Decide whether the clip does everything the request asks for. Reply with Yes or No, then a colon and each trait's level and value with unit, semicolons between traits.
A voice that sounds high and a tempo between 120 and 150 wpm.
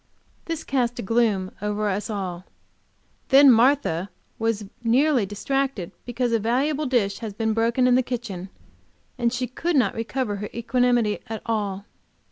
Yes: high, 230 Hz; average, 145 wpm